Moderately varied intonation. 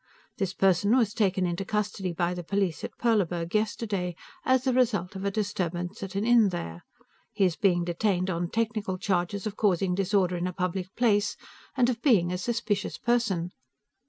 Yes: average, 3.3 semitones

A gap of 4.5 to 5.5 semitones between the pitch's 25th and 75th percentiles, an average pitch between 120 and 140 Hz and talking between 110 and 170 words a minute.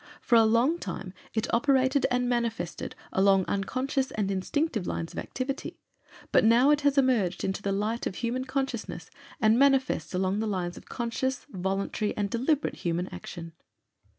No: average, 5.2 semitones; high, 230 Hz; average, 160 wpm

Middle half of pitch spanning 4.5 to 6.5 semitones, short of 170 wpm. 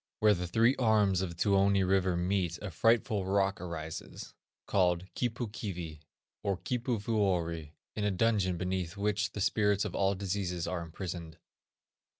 No: average, 2.9 semitones; average, 150 wpm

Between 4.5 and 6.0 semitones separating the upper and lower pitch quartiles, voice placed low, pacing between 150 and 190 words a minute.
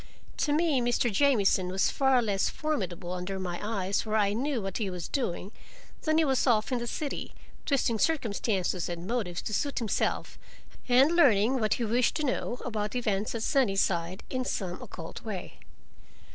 No: average, 5.1 semitones; high, 220 Hz; average, 170 wpm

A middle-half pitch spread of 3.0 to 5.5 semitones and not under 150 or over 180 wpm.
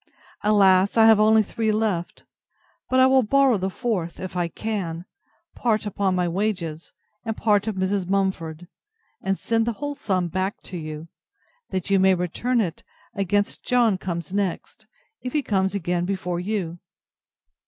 Yes: average, 3.5 semitones; average, 160 wpm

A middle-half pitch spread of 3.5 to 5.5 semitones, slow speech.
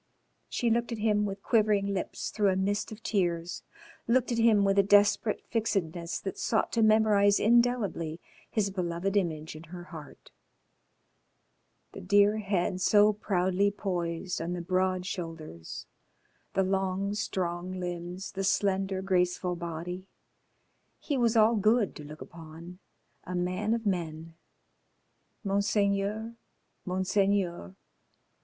No: average, 2.8 semitones; slow, 130 wpm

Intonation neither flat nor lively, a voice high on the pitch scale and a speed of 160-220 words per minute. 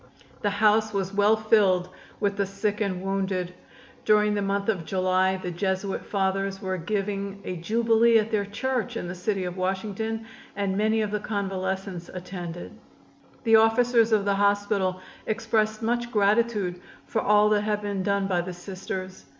No: narrow, 2.3 semitones; high, 200 Hz; average, 165 wpm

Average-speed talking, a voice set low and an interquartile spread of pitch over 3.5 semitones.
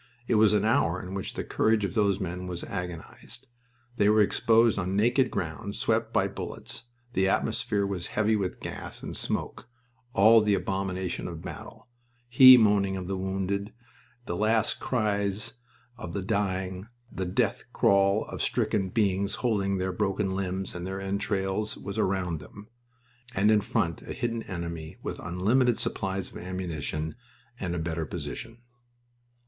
No: average, 155 wpm; very low, 95 Hz; narrow, 2.5 semitones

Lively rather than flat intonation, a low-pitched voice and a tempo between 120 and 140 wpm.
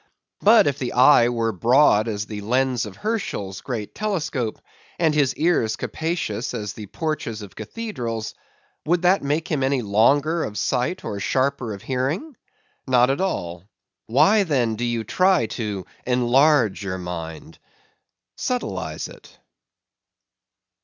Yes: wide, 6.2 semitones; low, 125 Hz; slow, 135 wpm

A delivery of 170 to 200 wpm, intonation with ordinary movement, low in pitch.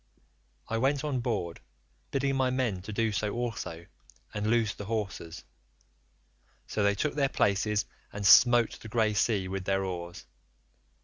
No: average, 150 wpm; average, 3.7 semitones; low, 105 Hz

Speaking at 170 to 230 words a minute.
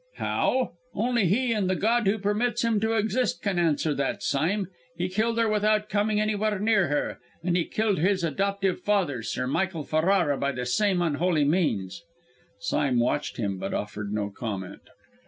Yes: average, 175 wpm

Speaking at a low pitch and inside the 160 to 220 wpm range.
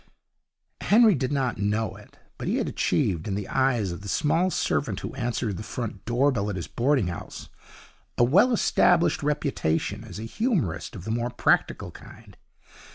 Yes: low, 120 Hz; average, 175 wpm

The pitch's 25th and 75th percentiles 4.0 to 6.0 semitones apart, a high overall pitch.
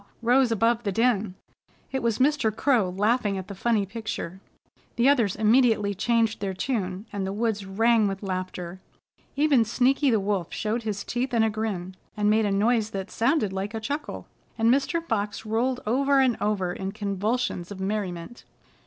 No: average, 3.4 semitones; high, 215 Hz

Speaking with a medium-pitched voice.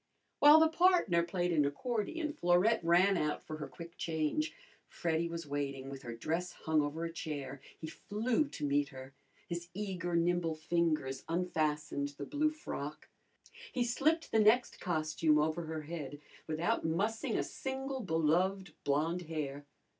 Yes: medium, 170 Hz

